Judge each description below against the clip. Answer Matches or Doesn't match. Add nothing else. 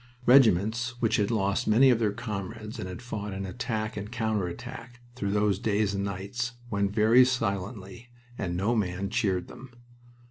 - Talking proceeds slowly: Doesn't match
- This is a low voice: Matches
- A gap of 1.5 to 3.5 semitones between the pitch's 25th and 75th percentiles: Matches